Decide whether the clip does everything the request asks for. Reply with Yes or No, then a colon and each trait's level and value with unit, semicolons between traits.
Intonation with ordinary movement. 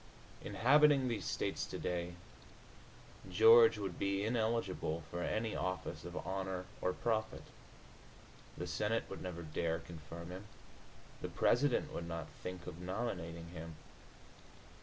Yes: average, 4.7 semitones